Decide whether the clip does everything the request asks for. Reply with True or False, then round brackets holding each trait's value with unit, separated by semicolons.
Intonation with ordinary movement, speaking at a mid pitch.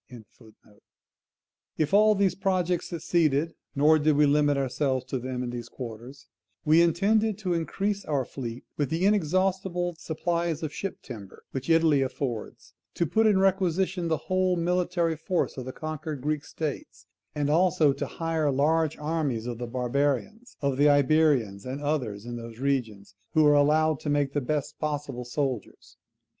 True (4.4 semitones; 150 Hz)